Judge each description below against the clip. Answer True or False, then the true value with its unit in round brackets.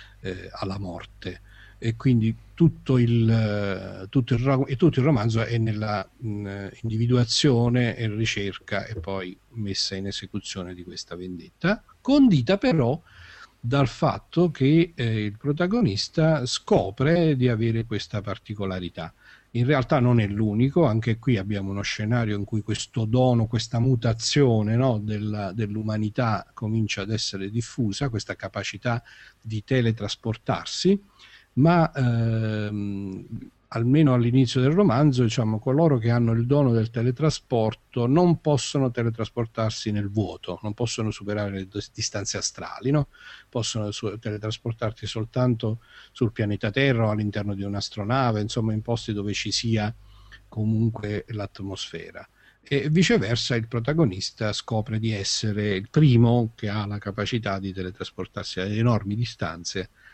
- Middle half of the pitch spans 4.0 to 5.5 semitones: False (3.4 semitones)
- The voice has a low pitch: True (110 Hz)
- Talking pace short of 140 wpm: True (130 wpm)